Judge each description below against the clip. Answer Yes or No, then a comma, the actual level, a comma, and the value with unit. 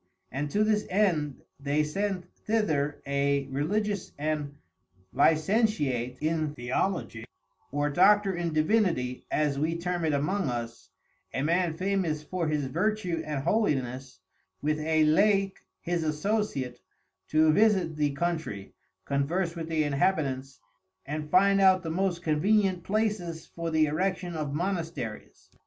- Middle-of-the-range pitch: Yes, medium, 160 Hz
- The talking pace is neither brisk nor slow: No, slow, 130 wpm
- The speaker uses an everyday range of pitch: Yes, average, 4.7 semitones